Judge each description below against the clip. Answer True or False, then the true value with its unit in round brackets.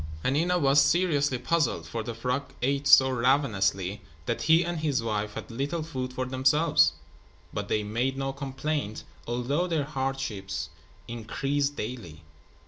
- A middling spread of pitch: True (4.0 semitones)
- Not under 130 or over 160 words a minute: True (140 wpm)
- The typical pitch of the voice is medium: False (130 Hz)